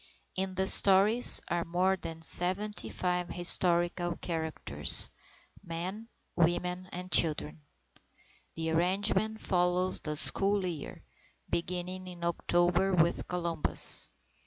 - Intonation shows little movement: Yes, narrow, 1.7 semitones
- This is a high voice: No, medium, 180 Hz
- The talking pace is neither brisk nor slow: No, slow, 100 wpm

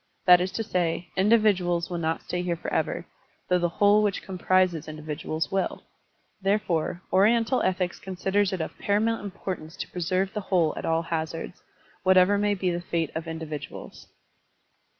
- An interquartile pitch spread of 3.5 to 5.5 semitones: No, average, 3.0 semitones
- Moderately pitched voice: Yes, medium, 180 Hz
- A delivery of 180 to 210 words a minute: No, average, 160 wpm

